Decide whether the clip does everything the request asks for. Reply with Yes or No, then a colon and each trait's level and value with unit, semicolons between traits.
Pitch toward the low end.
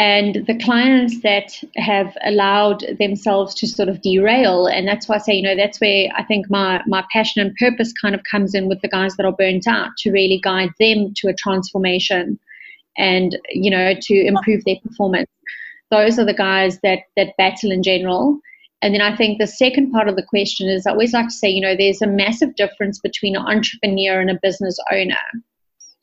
No: high, 200 Hz